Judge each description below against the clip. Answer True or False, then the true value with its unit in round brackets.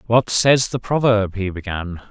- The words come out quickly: False (170 wpm)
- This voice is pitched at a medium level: False (110 Hz)